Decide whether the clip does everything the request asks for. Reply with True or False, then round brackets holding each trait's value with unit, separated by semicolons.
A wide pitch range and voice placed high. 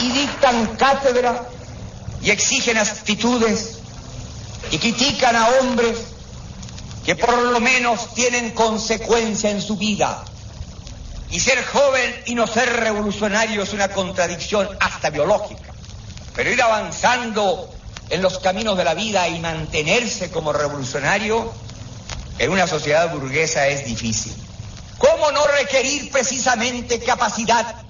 True (7.2 semitones; 215 Hz)